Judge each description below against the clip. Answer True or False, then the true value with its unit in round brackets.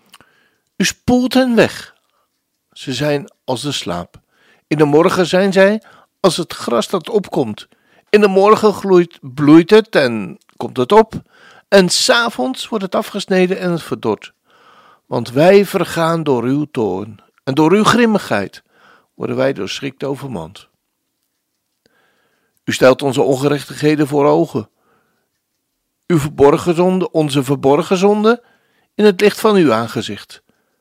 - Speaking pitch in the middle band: True (170 Hz)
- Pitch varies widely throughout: True (6.3 semitones)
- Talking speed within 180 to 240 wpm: False (135 wpm)